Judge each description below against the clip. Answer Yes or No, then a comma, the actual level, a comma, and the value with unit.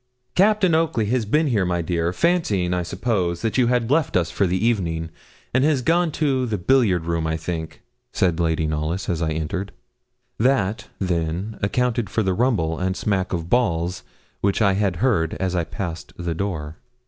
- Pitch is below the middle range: Yes, very low, 95 Hz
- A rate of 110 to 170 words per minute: No, average, 185 wpm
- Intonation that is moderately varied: No, wide, 6.1 semitones